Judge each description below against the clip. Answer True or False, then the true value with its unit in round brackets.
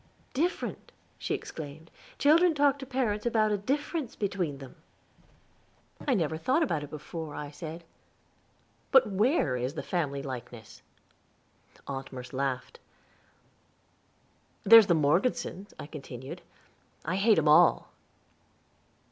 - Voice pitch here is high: False (175 Hz)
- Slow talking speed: True (120 wpm)